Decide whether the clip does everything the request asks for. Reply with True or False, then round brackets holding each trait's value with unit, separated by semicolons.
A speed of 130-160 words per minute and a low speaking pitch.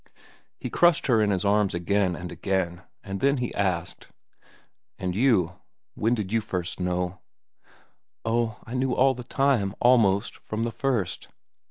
True (155 wpm; 105 Hz)